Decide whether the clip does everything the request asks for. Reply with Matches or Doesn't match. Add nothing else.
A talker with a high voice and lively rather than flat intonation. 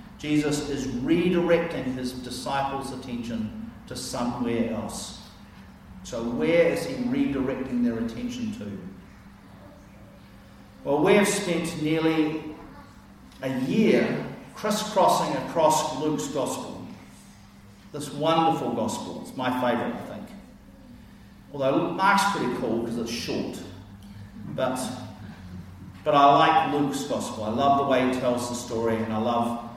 Doesn't match